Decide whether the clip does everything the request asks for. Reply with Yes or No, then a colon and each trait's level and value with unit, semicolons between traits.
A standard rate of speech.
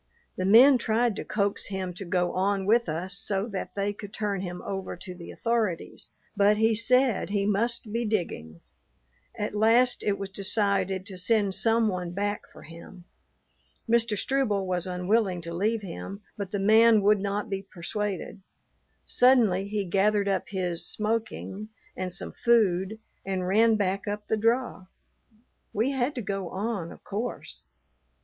Yes: average, 160 wpm